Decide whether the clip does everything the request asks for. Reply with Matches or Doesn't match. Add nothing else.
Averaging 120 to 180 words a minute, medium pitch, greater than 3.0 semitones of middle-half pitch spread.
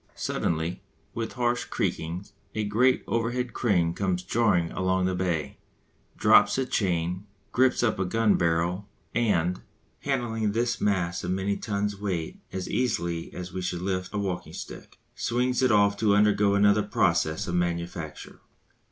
Doesn't match